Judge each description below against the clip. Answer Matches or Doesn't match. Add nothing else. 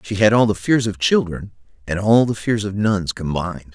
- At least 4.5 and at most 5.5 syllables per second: Matches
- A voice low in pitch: Matches